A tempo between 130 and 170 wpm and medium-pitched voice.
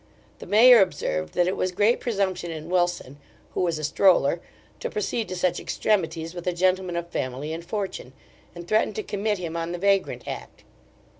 No: average, 190 wpm; medium, 180 Hz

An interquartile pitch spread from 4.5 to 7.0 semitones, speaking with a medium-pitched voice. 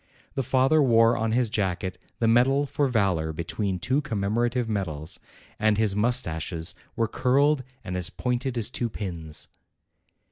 No: average, 5.2 semitones; low, 115 Hz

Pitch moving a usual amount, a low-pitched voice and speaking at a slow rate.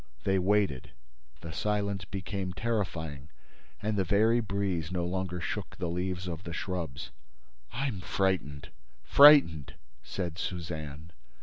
Yes: average, 3.9 semitones; very low, 90 Hz; slow, 115 wpm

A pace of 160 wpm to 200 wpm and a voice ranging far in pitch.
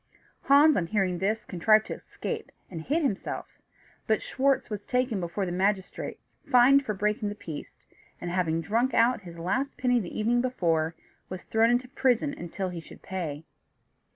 Yes: average, 170 wpm; wide, 5.7 semitones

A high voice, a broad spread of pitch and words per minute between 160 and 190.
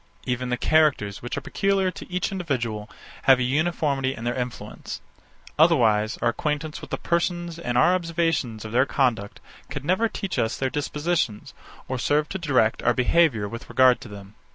No: low, 135 Hz; wide, 5.9 semitones; average, 175 wpm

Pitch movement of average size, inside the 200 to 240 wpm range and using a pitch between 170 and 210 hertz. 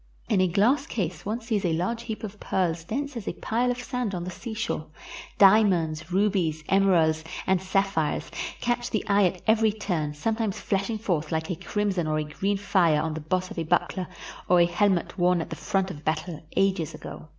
Yes: average, 4.3 semitones; fast, 205 wpm; high, 190 Hz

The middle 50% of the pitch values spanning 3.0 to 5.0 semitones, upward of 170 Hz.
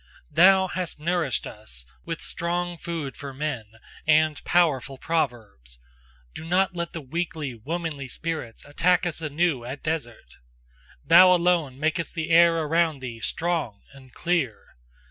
No: average, 4.4 semitones; medium, 160 Hz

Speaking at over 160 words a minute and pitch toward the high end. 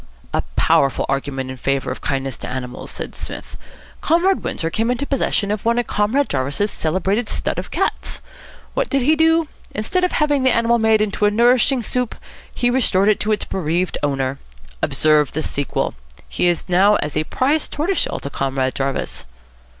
Yes: average, 180 wpm; high, 205 Hz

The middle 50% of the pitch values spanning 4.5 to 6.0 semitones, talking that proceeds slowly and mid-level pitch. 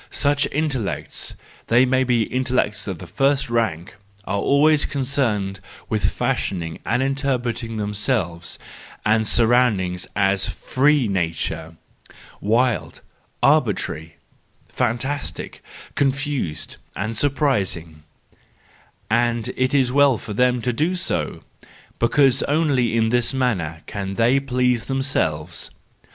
No: average, 5.2 semitones; slow, 110 wpm; low, 120 Hz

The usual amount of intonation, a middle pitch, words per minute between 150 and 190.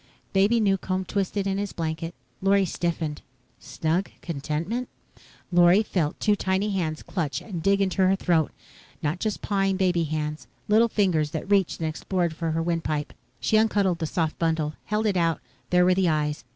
Yes: average, 3.6 semitones; medium, 180 Hz; average, 170 wpm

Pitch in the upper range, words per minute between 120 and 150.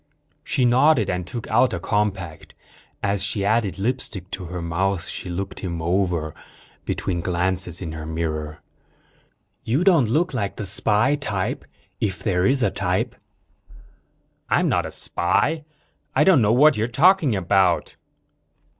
No: low, 100 Hz; average, 145 wpm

